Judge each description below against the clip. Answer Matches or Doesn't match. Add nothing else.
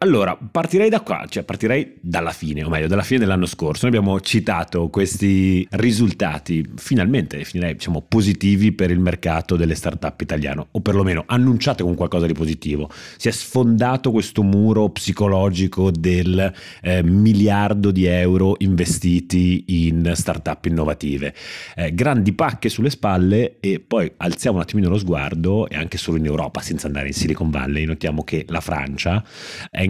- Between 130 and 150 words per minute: Doesn't match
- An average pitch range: Matches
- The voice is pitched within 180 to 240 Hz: Doesn't match